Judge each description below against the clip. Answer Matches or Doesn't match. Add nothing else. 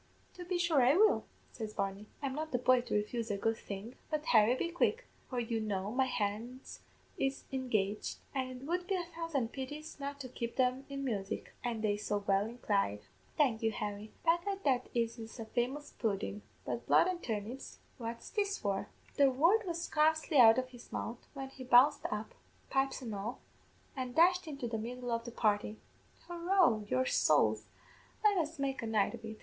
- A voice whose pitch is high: Matches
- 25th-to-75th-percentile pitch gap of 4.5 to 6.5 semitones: Matches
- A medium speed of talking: Matches